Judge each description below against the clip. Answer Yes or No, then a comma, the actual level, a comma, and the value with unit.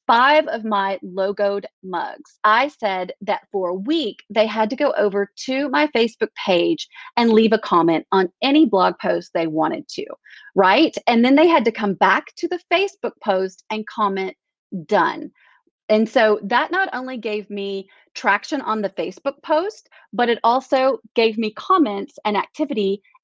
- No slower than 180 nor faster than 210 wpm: No, average, 170 wpm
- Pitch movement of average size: No, wide, 7.1 semitones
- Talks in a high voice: Yes, high, 225 Hz